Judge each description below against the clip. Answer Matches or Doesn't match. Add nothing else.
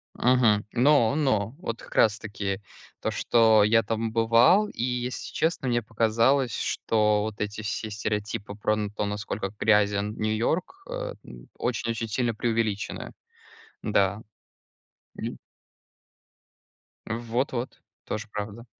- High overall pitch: Doesn't match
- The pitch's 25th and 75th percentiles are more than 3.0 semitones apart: Doesn't match